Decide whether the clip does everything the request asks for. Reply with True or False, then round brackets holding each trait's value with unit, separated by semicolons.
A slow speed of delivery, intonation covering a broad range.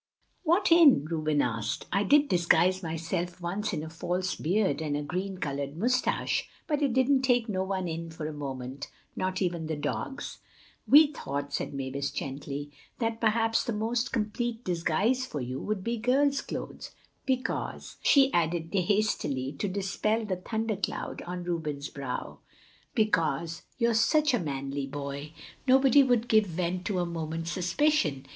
False (150 wpm; 7.0 semitones)